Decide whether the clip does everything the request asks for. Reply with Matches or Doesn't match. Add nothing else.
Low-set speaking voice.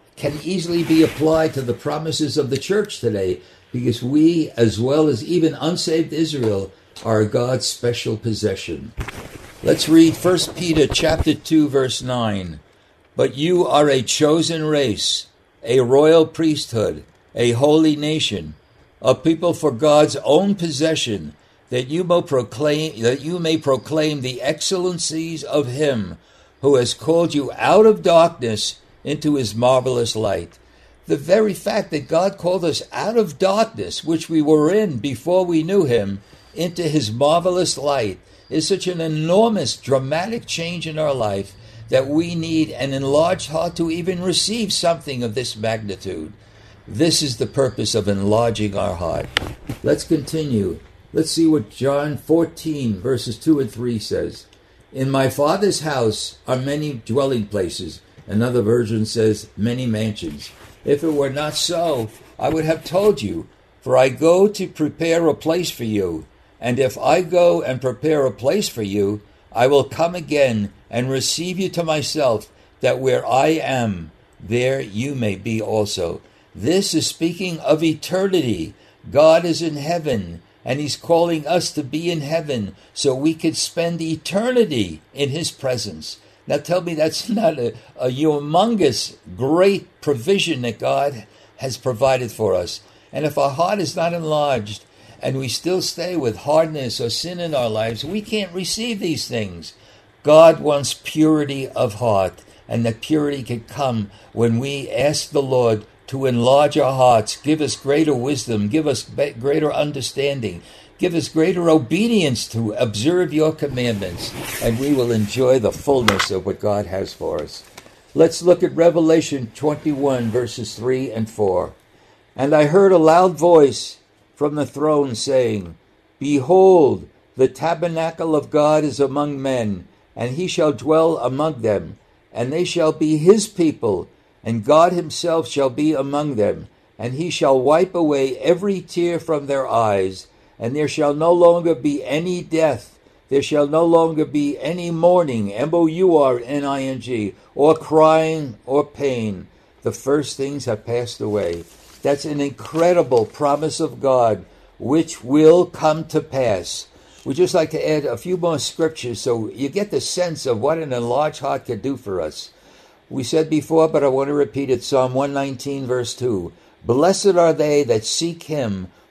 Doesn't match